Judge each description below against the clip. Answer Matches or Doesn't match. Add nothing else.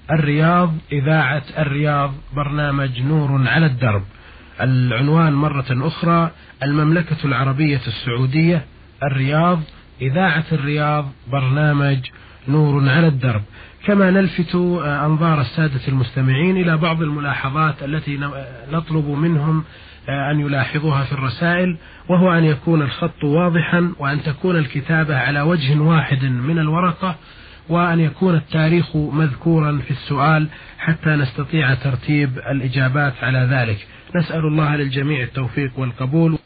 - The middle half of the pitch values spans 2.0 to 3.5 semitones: Matches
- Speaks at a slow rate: Doesn't match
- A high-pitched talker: Doesn't match